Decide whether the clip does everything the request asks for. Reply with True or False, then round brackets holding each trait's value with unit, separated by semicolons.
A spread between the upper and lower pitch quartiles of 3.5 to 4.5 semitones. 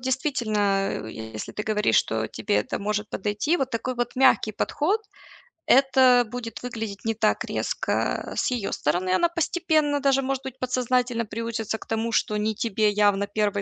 True (3.9 semitones)